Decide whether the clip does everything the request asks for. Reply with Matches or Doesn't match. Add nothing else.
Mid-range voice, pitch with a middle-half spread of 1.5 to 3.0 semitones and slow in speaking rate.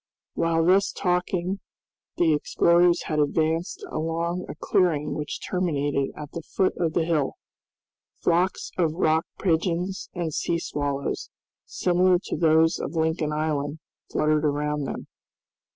Matches